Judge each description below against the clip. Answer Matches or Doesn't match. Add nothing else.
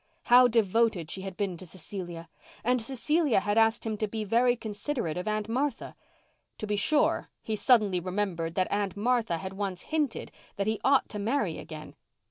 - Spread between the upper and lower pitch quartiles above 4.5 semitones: Doesn't match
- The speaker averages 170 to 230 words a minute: Matches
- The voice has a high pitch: Matches